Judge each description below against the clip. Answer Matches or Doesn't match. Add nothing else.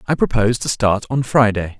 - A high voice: Doesn't match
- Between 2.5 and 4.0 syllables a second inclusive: Doesn't match